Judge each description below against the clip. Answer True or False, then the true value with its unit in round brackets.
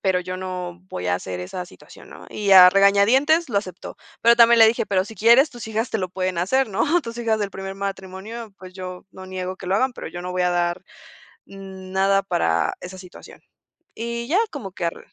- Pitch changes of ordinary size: True (3.6 semitones)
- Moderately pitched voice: False (195 Hz)